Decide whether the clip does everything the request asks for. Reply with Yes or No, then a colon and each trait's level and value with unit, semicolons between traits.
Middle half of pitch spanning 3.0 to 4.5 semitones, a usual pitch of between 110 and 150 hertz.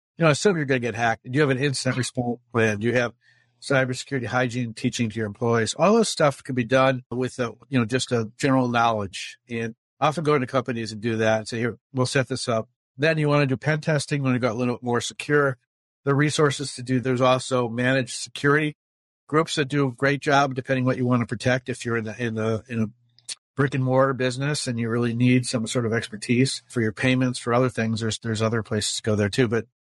No: narrow, 2.5 semitones; low, 125 Hz